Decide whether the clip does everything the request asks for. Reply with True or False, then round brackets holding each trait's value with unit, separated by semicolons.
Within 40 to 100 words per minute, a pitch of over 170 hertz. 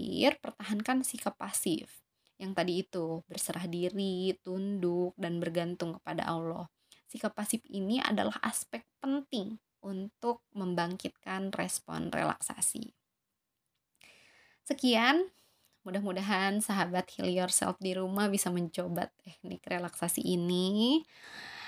True (95 wpm; 190 Hz)